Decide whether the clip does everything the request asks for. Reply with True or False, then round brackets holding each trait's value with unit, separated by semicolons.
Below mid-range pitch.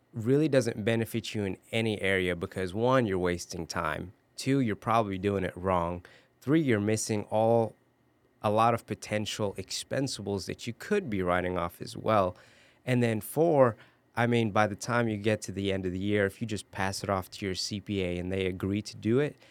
True (105 Hz)